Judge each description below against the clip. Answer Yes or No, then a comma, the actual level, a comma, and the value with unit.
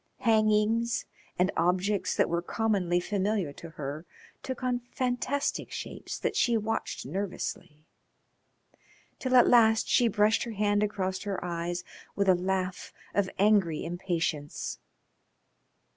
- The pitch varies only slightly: No, average, 4.0 semitones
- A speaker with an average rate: No, slow, 125 wpm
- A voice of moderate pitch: No, high, 200 Hz